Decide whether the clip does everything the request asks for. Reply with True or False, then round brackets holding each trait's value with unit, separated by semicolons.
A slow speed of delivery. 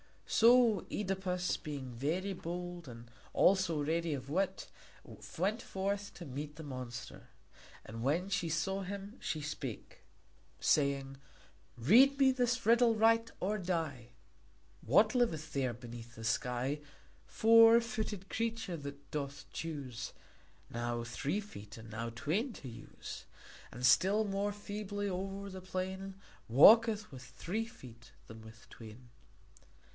True (130 wpm)